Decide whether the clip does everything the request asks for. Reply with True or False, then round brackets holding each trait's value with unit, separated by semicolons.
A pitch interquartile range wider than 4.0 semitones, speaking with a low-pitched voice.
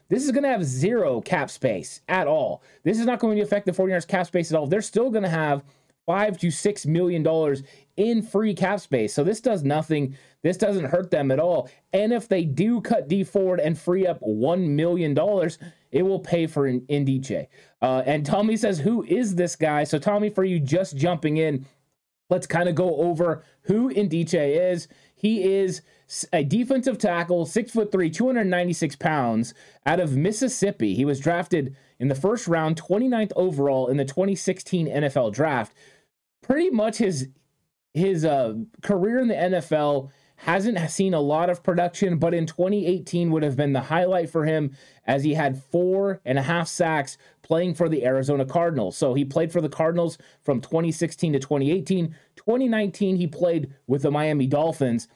False (4.7 semitones; 170 Hz)